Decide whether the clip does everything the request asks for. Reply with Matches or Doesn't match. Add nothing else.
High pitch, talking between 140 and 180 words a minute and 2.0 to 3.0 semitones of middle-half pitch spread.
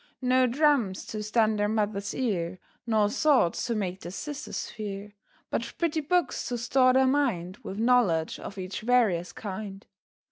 Doesn't match